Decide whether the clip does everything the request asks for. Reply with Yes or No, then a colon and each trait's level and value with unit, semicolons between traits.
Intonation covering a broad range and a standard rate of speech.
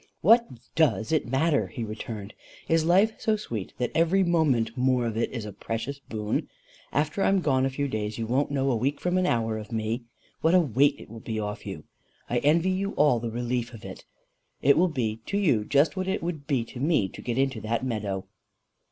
No: wide, 6.1 semitones; fast, 220 wpm